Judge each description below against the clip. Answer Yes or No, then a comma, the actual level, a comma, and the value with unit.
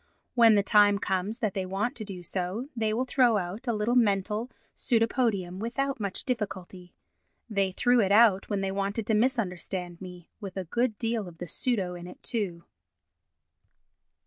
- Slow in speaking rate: No, average, 170 wpm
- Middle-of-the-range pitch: No, high, 205 Hz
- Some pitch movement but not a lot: Yes, average, 3.7 semitones